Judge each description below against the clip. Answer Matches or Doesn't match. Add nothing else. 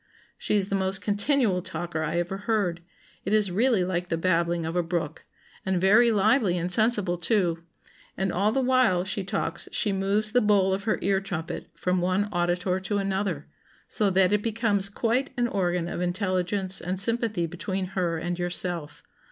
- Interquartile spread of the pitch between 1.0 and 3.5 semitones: Matches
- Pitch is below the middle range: Doesn't match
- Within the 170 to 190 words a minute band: Matches